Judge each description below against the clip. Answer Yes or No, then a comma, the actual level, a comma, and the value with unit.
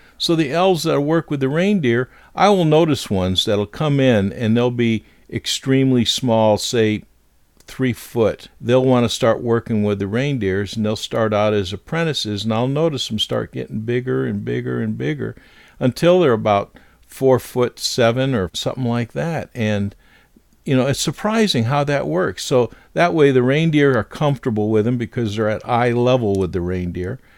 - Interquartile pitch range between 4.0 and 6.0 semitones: Yes, average, 4.3 semitones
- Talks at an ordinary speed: Yes, average, 180 wpm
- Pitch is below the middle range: Yes, low, 120 Hz